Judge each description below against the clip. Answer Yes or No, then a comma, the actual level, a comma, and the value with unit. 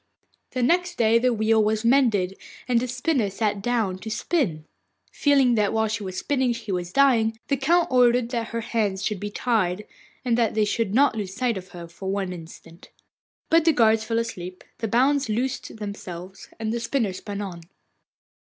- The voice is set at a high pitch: Yes, high, 225 Hz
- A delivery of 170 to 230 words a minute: Yes, average, 190 wpm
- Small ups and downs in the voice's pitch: No, average, 3.9 semitones